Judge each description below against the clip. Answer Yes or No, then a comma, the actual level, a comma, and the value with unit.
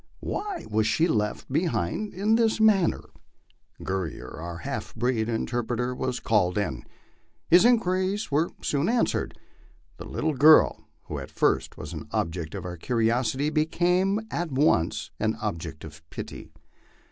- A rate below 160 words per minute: Yes, average, 145 wpm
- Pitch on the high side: No, low, 125 Hz